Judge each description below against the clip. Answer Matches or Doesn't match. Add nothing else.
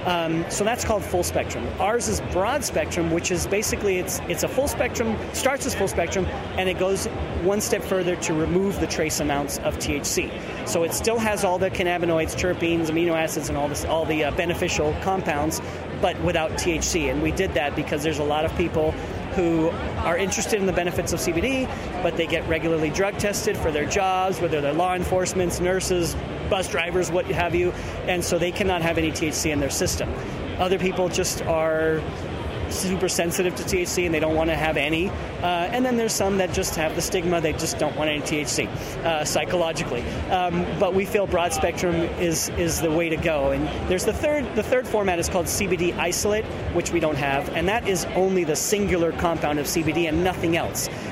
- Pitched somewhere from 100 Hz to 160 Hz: Doesn't match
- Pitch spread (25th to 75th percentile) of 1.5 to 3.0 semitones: Matches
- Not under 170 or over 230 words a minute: Matches